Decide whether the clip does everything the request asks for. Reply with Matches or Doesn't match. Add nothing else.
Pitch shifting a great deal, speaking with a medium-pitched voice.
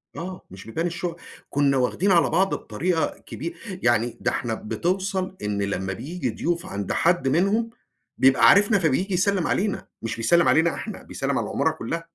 Matches